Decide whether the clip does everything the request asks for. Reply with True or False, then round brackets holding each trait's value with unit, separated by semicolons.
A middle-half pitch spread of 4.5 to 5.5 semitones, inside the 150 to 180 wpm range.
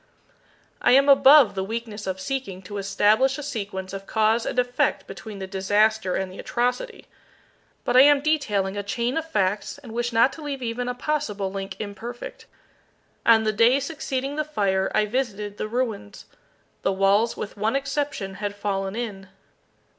True (4.9 semitones; 170 wpm)